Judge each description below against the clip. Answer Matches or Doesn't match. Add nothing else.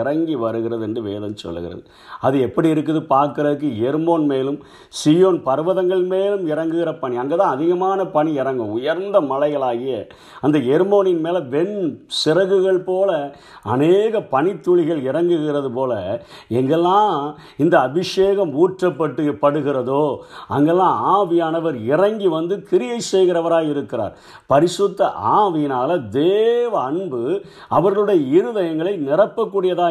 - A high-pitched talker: Doesn't match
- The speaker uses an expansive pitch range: Doesn't match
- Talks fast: Doesn't match